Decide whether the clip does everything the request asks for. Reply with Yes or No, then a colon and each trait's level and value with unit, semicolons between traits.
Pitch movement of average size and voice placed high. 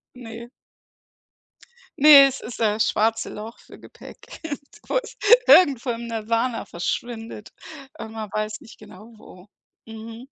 No: narrow, 2.0 semitones; high, 225 Hz